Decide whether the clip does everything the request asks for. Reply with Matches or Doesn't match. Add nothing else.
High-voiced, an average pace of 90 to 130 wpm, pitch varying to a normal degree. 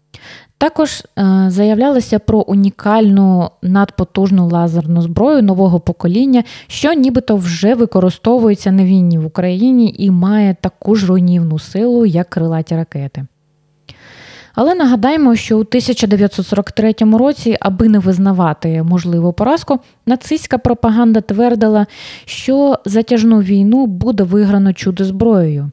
Matches